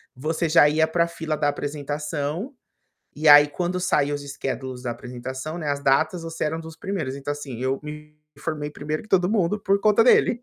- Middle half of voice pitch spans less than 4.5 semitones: Yes, average, 2.9 semitones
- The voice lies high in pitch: No, medium, 150 Hz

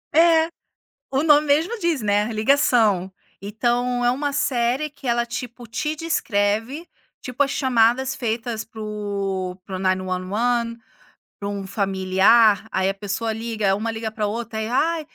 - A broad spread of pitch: No, average, 4.3 semitones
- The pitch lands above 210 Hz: Yes, high, 230 Hz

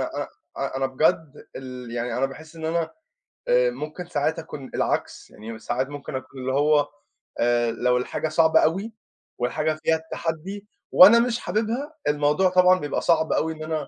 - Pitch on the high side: No, medium, 155 Hz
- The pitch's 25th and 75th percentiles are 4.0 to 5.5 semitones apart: Yes, average, 4.9 semitones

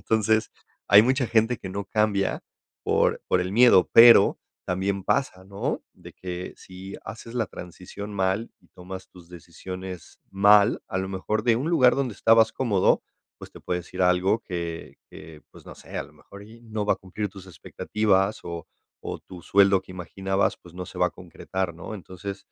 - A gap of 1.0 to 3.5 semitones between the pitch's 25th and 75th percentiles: Yes, average, 2.9 semitones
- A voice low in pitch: Yes, very low, 95 Hz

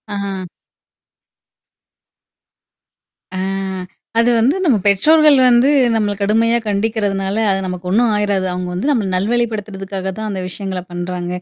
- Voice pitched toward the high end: Yes, high, 200 Hz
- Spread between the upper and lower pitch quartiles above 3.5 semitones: No, average, 3.0 semitones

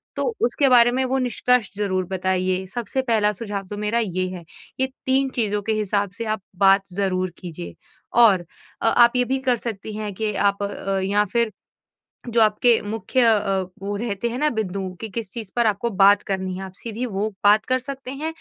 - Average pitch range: Yes, average, 3.5 semitones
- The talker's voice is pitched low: No, high, 210 Hz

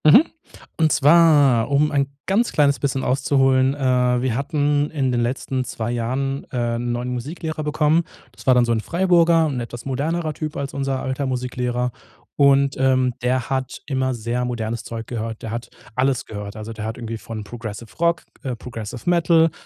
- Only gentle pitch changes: No, average, 3.4 semitones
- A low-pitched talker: Yes, low, 130 Hz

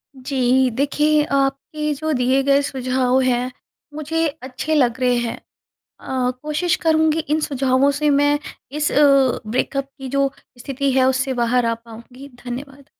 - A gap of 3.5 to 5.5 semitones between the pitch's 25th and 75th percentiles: No, narrow, 2.5 semitones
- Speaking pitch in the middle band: No, very high, 270 Hz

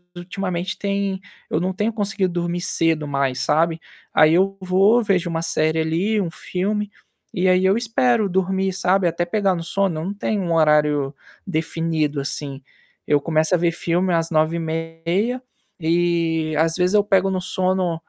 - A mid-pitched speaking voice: Yes, medium, 175 Hz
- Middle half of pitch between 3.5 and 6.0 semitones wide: No, average, 2.9 semitones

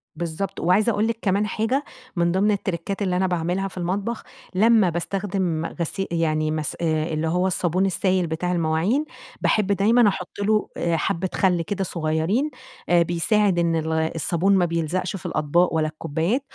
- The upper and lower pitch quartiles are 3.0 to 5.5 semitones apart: Yes, average, 3.3 semitones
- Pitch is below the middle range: No, medium, 180 Hz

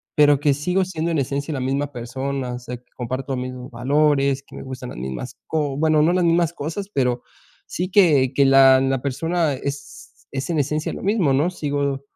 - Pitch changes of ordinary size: Yes, average, 3.2 semitones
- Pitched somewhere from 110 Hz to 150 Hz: Yes, medium, 140 Hz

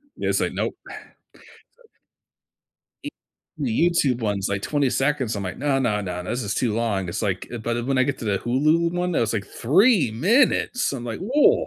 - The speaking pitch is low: Yes, low, 120 Hz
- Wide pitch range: Yes, wide, 6.0 semitones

